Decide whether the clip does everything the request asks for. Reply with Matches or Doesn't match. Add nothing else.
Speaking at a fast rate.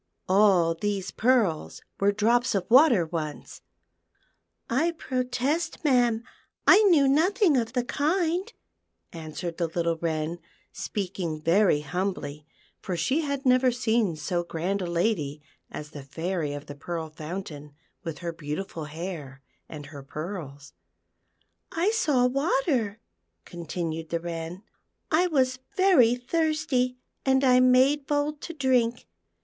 Doesn't match